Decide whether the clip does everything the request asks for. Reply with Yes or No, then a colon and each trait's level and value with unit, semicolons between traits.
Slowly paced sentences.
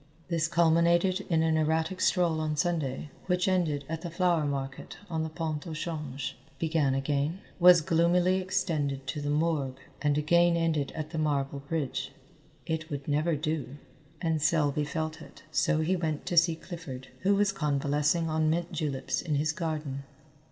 No: average, 165 wpm